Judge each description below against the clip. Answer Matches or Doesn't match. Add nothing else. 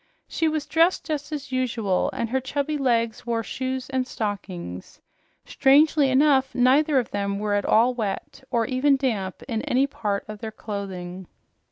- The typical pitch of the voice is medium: Doesn't match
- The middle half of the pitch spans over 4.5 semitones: Matches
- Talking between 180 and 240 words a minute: Doesn't match